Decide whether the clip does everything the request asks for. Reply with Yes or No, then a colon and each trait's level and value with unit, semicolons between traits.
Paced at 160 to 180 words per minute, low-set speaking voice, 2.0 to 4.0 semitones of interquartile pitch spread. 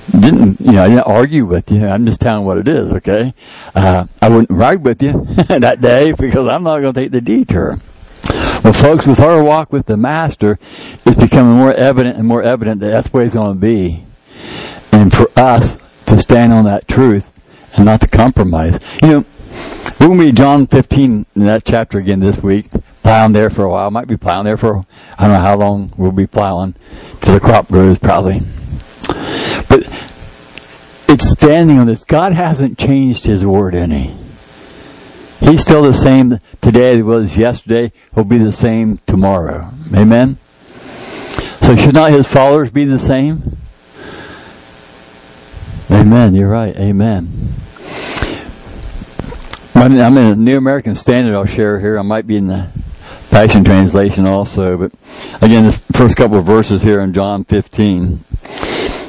No: average, 170 wpm; low, 110 Hz; average, 4.4 semitones